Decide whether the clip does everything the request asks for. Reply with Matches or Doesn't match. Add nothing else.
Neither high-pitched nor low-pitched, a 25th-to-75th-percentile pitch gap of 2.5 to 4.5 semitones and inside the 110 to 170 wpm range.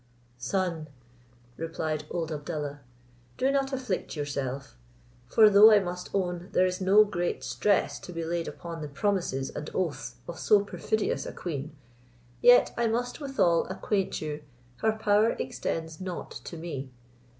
Doesn't match